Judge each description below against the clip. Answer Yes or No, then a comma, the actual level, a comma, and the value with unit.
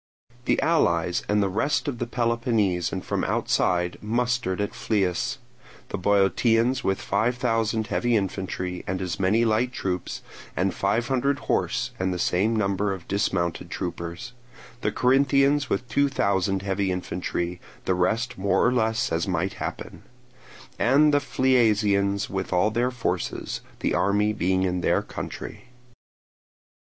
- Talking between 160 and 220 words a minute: No, average, 140 wpm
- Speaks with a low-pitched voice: Yes, low, 100 Hz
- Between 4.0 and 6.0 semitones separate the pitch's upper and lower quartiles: Yes, average, 4.5 semitones